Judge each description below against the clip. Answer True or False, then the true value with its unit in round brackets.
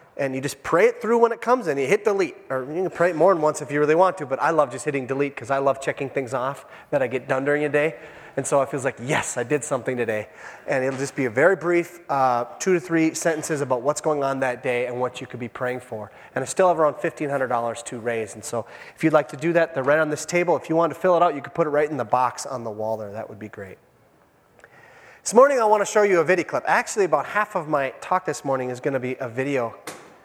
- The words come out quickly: True (295 wpm)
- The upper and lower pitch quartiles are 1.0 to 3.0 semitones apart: False (4.9 semitones)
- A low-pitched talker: False (145 Hz)